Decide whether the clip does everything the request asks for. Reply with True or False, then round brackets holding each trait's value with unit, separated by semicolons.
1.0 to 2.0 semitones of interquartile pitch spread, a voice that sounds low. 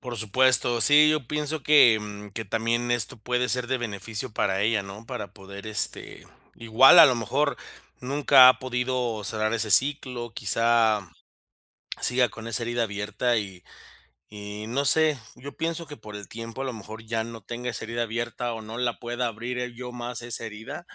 False (2.5 semitones; 120 Hz)